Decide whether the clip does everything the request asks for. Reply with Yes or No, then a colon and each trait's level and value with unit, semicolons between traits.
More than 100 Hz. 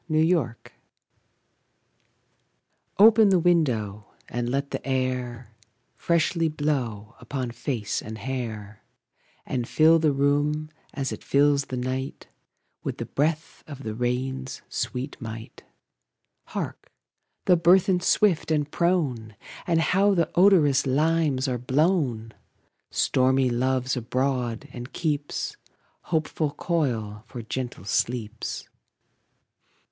Yes: low, 135 Hz